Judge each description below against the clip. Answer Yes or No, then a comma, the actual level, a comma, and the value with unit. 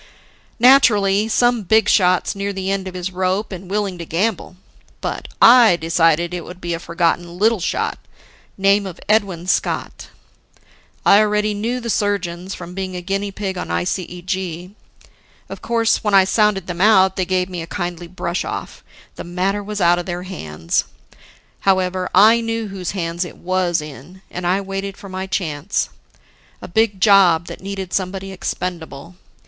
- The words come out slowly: No, average, 170 wpm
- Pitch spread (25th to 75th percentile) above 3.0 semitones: No, narrow, 2.4 semitones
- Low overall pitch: No, high, 190 Hz